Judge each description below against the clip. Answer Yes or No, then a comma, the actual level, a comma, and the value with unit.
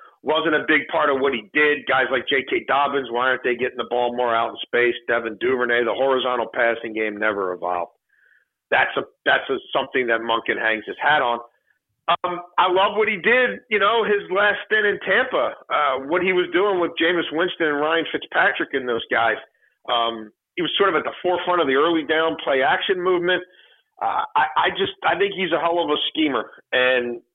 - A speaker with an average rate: No, fast, 210 wpm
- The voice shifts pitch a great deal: Yes, wide, 7.4 semitones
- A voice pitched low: No, medium, 165 Hz